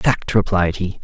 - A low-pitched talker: Yes, very low, 95 Hz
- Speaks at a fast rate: No, average, 175 wpm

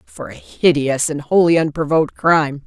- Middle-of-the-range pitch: Yes, medium, 155 Hz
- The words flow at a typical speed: Yes, average, 155 wpm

